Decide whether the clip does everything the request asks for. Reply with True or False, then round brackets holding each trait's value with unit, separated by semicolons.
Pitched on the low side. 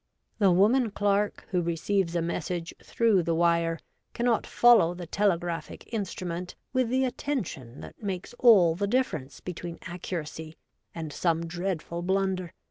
False (180 Hz)